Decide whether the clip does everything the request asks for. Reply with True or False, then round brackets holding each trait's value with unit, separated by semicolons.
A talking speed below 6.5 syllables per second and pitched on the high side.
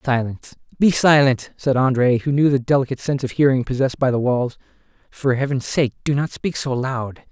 False (5.8 syllables/s; 130 Hz)